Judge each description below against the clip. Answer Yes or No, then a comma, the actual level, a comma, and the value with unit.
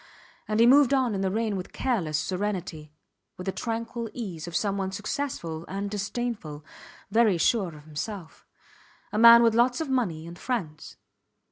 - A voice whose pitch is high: Yes, high, 205 Hz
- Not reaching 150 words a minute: No, average, 160 wpm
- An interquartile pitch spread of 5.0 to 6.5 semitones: Yes, wide, 5.4 semitones